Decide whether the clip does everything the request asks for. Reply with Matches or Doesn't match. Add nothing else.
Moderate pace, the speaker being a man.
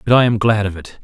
Doesn't match